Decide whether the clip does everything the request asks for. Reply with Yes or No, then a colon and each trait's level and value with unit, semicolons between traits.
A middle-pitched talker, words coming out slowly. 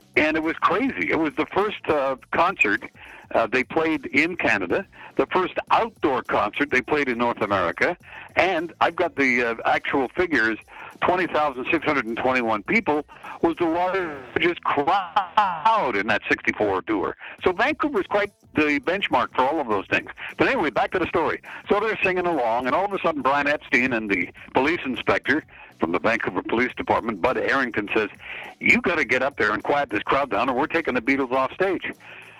No: medium, 150 Hz; average, 190 wpm